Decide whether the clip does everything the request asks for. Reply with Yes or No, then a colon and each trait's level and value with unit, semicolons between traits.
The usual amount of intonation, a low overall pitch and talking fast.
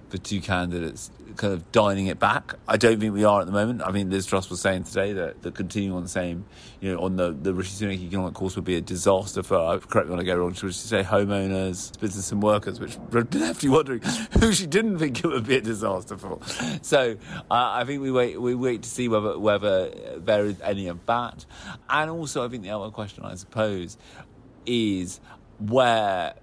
Yes: average, 3.7 semitones; low, 100 Hz; fast, 220 wpm